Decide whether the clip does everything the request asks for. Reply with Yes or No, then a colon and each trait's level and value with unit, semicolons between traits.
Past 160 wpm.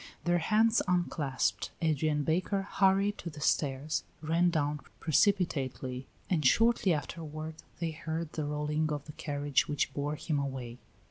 No: average, 140 wpm